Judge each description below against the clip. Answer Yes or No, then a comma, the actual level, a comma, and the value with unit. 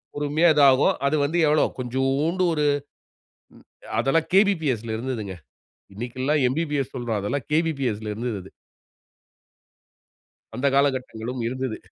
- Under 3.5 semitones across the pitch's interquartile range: No, average, 3.8 semitones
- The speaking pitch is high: No, low, 135 Hz